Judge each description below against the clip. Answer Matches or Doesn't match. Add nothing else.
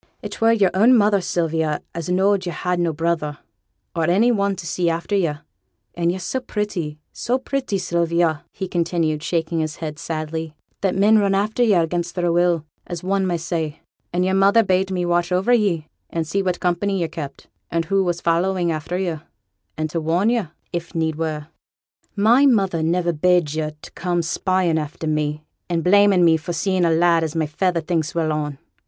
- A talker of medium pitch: Matches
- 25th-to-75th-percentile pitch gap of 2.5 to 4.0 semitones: Matches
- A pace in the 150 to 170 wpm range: Doesn't match